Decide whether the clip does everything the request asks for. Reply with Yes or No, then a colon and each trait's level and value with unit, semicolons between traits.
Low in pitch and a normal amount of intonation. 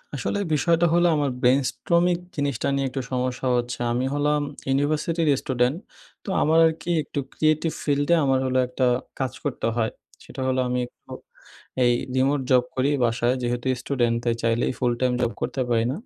Yes: low, 130 Hz; average, 3.1 semitones